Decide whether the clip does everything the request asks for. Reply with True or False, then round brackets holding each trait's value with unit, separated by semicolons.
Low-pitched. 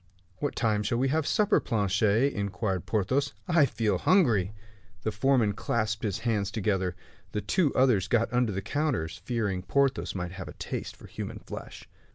True (110 Hz)